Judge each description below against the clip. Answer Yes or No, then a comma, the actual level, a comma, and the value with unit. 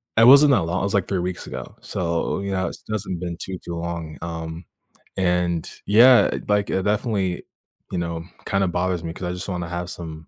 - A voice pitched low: Yes, very low, 90 Hz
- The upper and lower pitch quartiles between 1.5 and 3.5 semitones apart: Yes, narrow, 2.6 semitones